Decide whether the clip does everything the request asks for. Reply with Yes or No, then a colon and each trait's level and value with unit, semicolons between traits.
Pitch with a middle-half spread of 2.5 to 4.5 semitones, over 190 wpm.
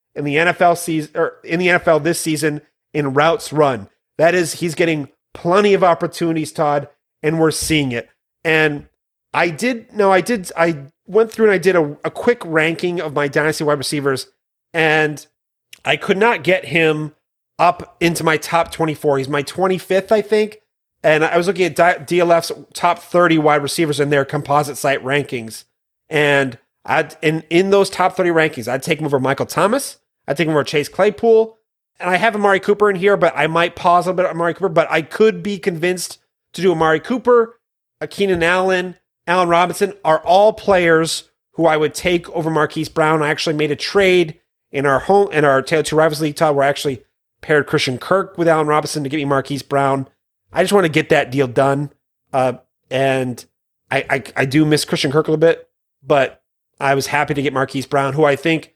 Yes: average, 3.6 semitones; average, 200 wpm